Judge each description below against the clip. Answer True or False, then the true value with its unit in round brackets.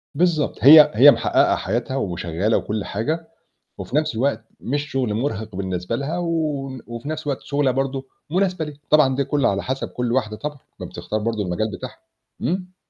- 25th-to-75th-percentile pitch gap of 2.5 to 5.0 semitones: False (5.4 semitones)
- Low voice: True (130 Hz)